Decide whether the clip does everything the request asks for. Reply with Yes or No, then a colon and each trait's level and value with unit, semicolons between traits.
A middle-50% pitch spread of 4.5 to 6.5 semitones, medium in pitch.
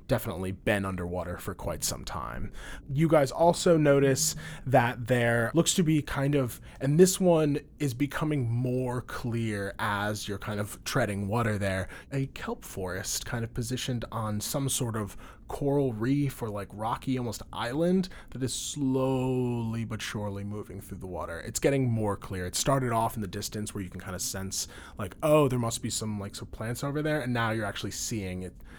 No: average, 5.0 semitones; low, 120 Hz